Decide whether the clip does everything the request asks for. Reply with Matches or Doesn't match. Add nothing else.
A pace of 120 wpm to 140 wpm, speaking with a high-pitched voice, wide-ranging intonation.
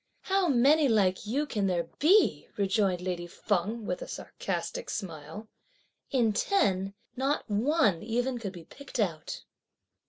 Matches